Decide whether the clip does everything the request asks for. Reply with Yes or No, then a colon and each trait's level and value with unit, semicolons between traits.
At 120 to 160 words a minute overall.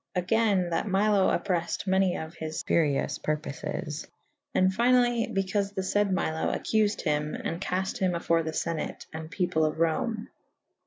Yes: average, 155 wpm